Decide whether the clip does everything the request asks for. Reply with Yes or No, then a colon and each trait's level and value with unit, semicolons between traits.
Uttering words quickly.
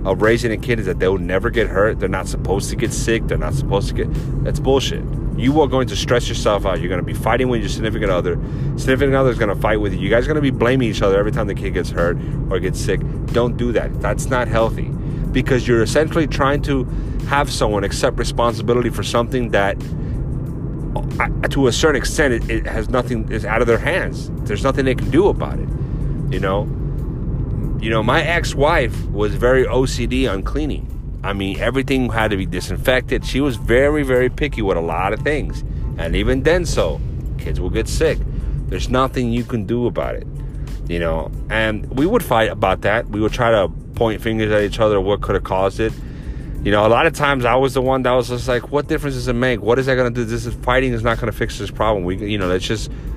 Yes: fast, 235 wpm